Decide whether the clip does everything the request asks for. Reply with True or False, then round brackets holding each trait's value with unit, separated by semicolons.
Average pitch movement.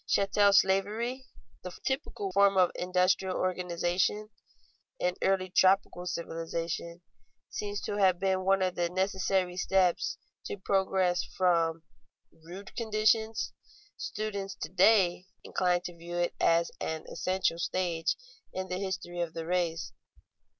False (1.9 semitones)